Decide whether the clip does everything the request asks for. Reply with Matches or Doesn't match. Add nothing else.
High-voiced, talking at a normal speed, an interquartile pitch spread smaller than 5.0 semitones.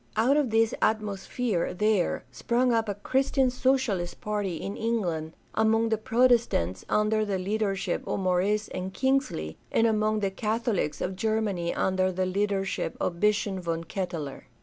Matches